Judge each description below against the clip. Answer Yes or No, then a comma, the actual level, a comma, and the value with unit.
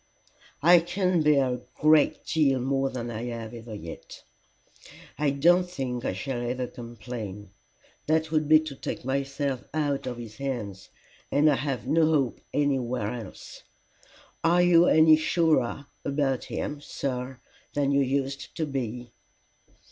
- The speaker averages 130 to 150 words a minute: Yes, average, 145 wpm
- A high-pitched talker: No, low, 135 Hz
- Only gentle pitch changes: No, average, 3.9 semitones